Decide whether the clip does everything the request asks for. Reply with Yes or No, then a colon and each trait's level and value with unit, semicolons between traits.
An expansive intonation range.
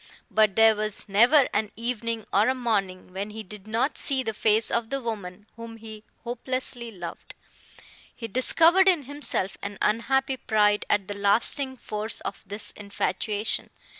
No: average, 3.1 semitones